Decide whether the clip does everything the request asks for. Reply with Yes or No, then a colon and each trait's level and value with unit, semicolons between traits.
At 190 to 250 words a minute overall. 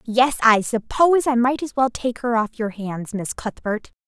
Yes: fast, 205 wpm